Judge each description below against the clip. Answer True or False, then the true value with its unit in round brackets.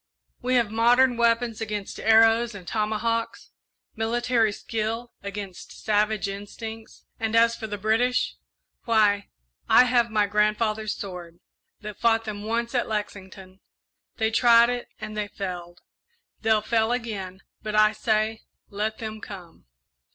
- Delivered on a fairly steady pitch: True (1.9 semitones)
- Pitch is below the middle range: False (220 Hz)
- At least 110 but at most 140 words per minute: True (135 wpm)